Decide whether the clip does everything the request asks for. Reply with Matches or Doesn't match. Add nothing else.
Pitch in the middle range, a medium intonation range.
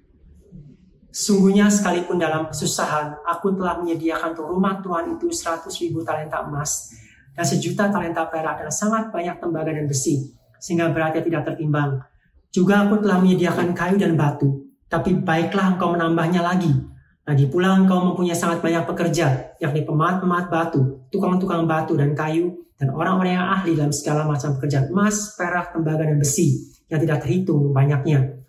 Matches